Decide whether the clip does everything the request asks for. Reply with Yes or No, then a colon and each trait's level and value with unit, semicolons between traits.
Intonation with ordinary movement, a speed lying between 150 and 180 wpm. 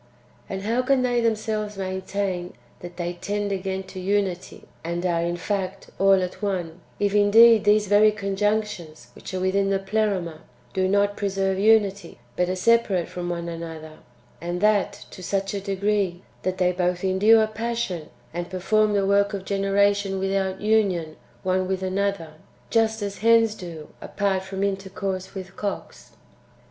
No: narrow, 2.1 semitones; average, 160 wpm